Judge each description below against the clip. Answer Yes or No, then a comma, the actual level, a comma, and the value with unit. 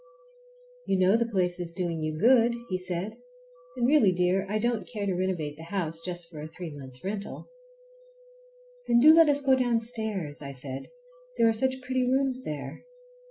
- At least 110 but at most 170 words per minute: No, average, 180 wpm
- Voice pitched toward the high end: Yes, high, 195 Hz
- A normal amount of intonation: No, wide, 6.1 semitones